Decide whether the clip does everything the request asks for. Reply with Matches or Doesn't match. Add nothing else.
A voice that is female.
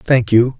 Doesn't match